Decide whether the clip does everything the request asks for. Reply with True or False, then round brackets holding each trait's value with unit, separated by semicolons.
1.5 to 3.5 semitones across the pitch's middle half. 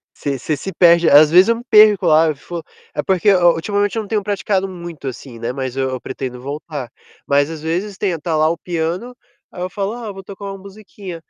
False (4.8 semitones)